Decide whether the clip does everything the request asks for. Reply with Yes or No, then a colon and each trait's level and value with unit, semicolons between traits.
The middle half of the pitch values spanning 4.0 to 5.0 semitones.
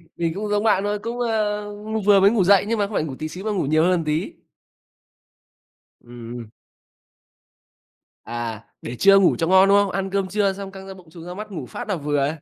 Yes: average, 4.6 semitones